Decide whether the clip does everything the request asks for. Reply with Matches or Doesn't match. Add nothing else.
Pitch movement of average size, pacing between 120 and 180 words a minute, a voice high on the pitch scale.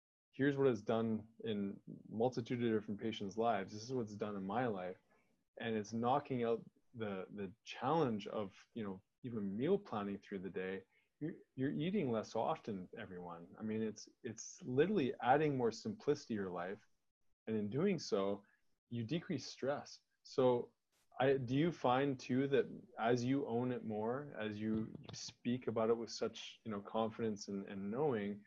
Doesn't match